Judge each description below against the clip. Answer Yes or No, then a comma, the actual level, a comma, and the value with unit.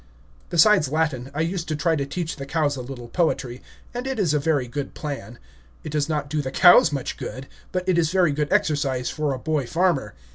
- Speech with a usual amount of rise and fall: Yes, average, 3.3 semitones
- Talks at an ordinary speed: No, fast, 220 wpm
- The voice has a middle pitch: Yes, medium, 150 Hz